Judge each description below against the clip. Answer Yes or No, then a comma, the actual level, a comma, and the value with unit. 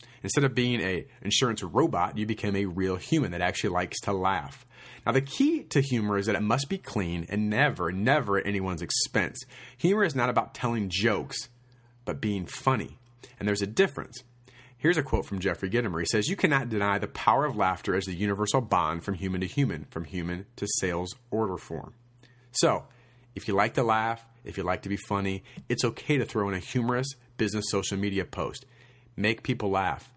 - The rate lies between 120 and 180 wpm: No, average, 200 wpm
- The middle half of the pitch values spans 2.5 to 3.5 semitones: No, average, 4.1 semitones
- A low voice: Yes, low, 115 Hz